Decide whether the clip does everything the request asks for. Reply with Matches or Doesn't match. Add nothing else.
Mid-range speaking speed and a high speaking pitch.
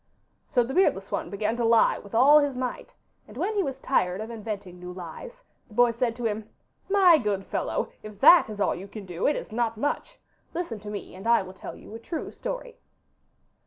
Doesn't match